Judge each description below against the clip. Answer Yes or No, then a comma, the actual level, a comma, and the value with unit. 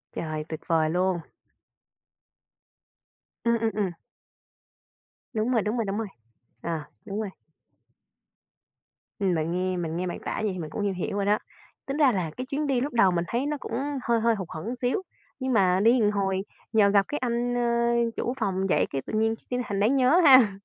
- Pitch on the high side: Yes, high, 215 Hz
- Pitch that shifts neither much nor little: Yes, average, 4.5 semitones